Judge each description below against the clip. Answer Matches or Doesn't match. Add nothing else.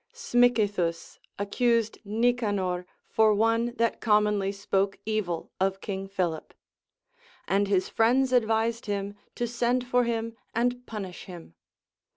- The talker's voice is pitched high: Matches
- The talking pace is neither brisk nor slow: Doesn't match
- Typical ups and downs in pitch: Matches